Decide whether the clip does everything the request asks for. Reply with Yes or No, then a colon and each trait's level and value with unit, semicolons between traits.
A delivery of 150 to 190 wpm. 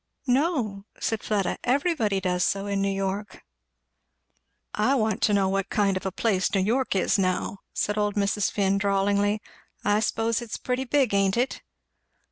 Yes: average, 165 wpm